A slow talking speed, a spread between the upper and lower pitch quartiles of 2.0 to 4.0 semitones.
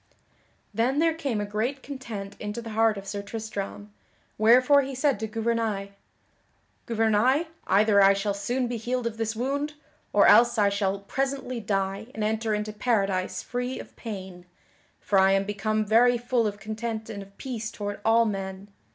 No: average, 170 wpm; average, 3.1 semitones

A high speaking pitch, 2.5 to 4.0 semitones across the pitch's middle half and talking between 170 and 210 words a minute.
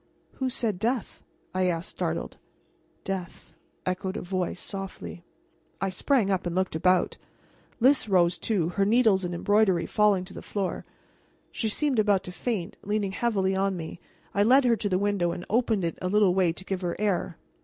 Yes: high, 195 Hz; average, 2.9 semitones; average, 185 wpm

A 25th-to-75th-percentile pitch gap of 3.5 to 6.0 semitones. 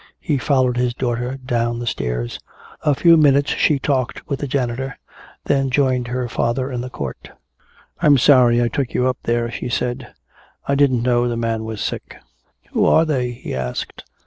No: narrow, 2.4 semitones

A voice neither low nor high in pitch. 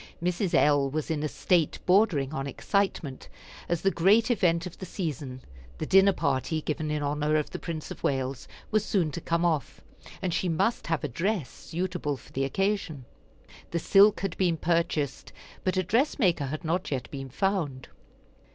Yes: medium, 165 Hz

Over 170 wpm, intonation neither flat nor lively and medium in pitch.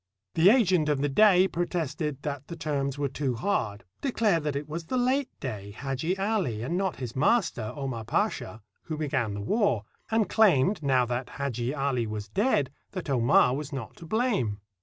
No: average, 180 wpm; wide, 6.5 semitones; medium, 145 Hz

